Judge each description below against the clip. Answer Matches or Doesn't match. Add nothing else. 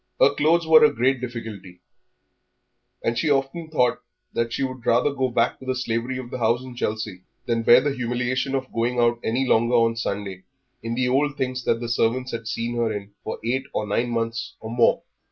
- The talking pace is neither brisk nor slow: Doesn't match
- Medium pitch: Doesn't match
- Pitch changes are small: Matches